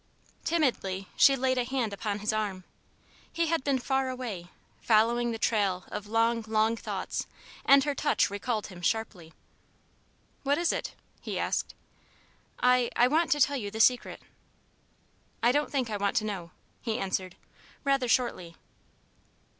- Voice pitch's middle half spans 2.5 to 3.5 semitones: No, average, 4.3 semitones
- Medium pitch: No, high, 230 Hz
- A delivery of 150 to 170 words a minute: Yes, average, 155 wpm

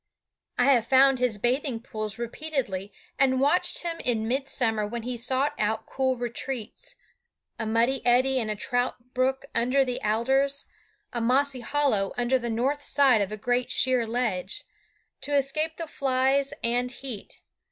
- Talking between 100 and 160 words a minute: Yes, average, 155 wpm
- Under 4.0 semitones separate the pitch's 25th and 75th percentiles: Yes, average, 2.8 semitones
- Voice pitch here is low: No, very high, 250 Hz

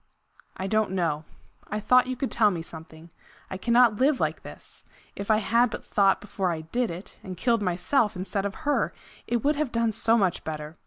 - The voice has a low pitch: No, high, 210 Hz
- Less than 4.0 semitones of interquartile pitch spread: No, average, 4.8 semitones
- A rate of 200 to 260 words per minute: Yes, fast, 205 wpm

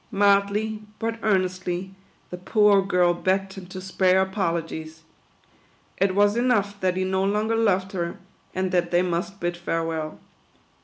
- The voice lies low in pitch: No, high, 190 Hz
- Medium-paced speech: Yes, average, 150 wpm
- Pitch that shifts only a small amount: Yes, narrow, 2.2 semitones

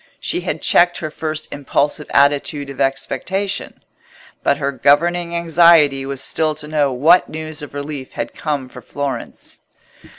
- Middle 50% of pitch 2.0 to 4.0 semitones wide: Yes, narrow, 2.6 semitones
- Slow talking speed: No, average, 145 wpm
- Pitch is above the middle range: No, medium, 150 Hz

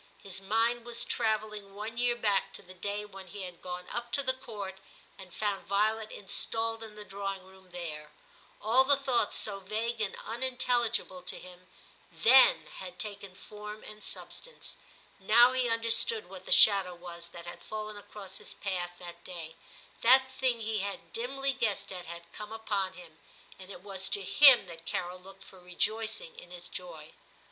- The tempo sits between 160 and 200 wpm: Yes, average, 175 wpm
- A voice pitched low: No, high, 205 Hz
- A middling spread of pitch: Yes, average, 3.9 semitones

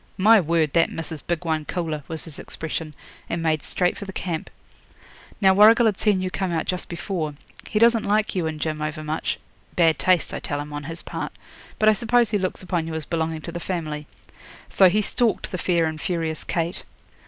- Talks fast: Yes, fast, 210 wpm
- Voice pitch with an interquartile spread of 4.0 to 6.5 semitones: No, average, 3.3 semitones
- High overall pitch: No, medium, 170 Hz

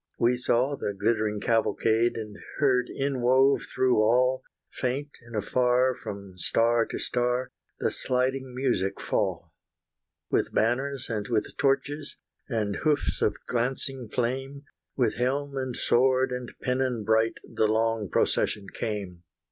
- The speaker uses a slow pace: Yes, slow, 130 wpm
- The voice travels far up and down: No, average, 2.8 semitones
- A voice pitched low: Yes, low, 125 Hz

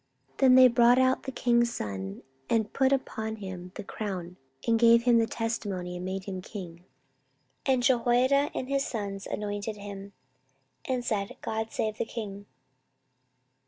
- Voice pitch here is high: Yes, high, 220 Hz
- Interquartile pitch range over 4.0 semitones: No, average, 3.7 semitones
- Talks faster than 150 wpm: Yes, average, 160 wpm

